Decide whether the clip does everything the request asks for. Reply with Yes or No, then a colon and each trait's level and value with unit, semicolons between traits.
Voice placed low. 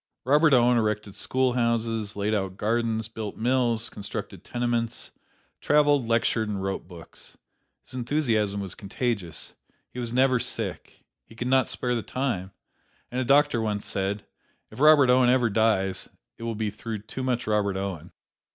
Yes: low, 115 Hz